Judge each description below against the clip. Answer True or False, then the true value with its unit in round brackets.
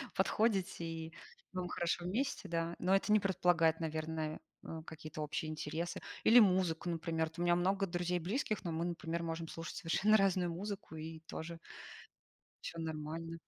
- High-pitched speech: False (170 Hz)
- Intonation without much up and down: True (2.3 semitones)